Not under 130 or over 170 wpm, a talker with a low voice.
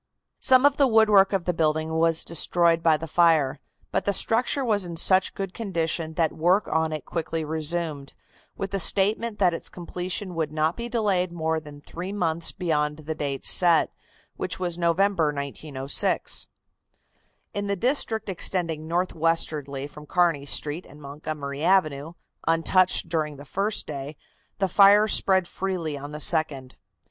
No: average, 160 wpm; medium, 165 Hz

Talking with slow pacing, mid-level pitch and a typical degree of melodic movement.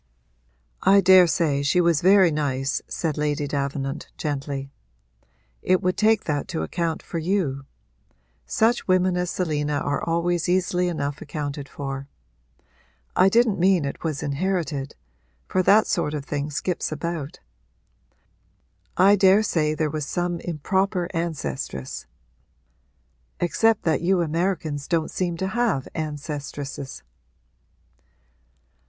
Yes: slow, 120 wpm; medium, 165 Hz; average, 4.2 semitones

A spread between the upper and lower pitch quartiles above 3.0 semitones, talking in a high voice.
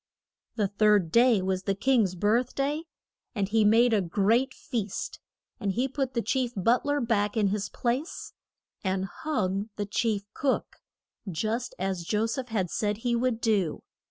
Yes: average, 3.8 semitones; high, 220 Hz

